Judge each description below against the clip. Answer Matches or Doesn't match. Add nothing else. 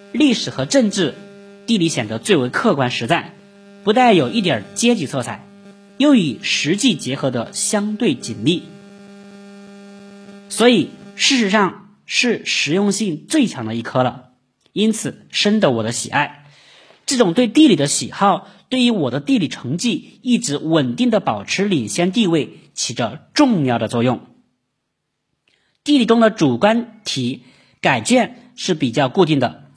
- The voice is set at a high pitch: Matches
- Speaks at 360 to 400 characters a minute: Doesn't match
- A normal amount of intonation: Doesn't match